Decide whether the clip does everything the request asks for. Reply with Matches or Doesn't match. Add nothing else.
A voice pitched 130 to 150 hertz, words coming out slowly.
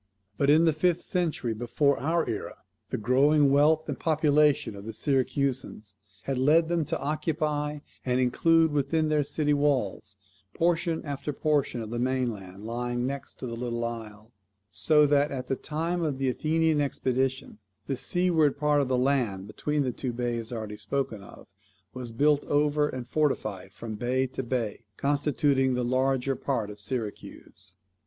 Doesn't match